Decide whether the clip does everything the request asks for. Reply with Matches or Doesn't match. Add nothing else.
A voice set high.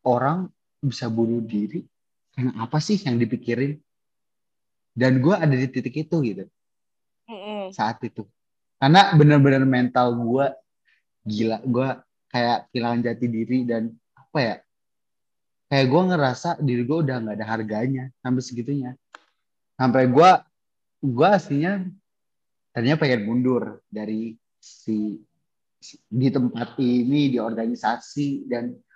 Doesn't match